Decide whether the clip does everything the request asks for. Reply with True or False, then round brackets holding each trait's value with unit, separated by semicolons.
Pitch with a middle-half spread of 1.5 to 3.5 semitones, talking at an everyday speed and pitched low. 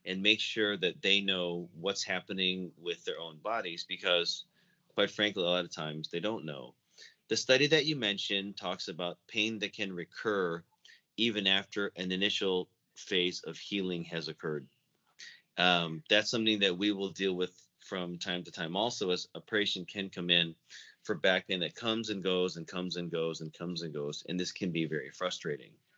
True (3.2 semitones; 190 wpm; 95 Hz)